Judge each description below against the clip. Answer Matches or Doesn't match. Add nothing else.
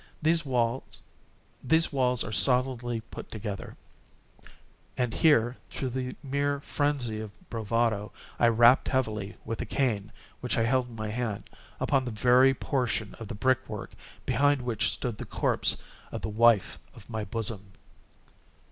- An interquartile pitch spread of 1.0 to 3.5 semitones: Matches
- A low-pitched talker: Matches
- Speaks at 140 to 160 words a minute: Matches